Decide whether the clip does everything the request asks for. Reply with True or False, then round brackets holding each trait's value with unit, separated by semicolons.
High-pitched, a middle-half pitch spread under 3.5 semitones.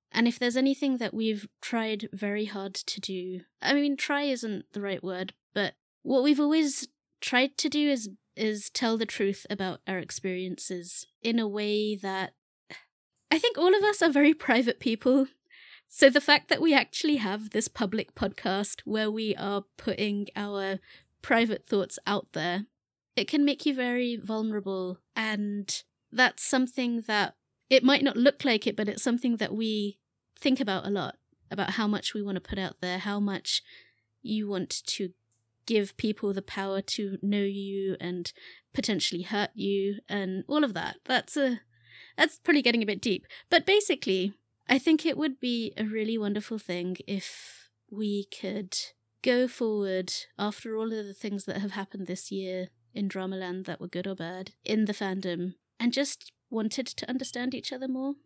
False (215 Hz; 4.5 semitones)